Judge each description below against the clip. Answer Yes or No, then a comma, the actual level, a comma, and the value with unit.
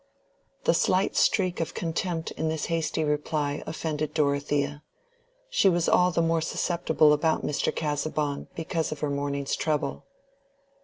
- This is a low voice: No, medium, 155 Hz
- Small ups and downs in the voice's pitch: Yes, narrow, 2.1 semitones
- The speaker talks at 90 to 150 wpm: Yes, average, 140 wpm